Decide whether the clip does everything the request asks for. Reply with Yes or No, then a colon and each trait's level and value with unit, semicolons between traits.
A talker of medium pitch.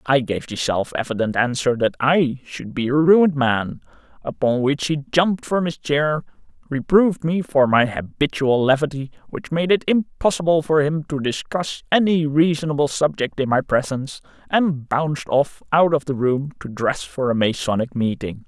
Yes: medium, 145 Hz